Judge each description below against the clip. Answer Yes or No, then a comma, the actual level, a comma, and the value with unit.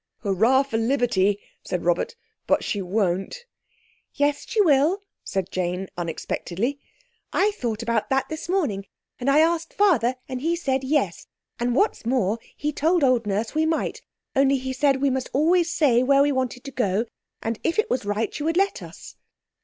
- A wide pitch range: Yes, wide, 5.7 semitones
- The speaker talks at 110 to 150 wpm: No, average, 175 wpm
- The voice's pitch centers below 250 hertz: No, very high, 260 Hz